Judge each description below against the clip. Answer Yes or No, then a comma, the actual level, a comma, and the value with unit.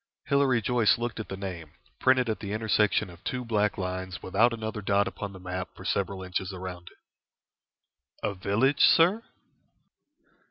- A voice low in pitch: Yes, low, 100 Hz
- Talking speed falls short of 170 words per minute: Yes, average, 160 wpm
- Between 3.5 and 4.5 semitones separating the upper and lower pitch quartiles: Yes, average, 4.0 semitones